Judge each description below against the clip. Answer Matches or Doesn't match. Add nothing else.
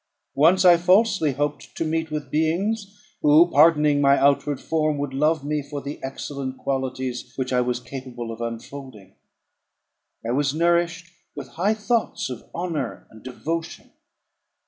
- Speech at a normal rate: Matches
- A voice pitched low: Doesn't match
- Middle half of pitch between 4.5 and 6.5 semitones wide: Doesn't match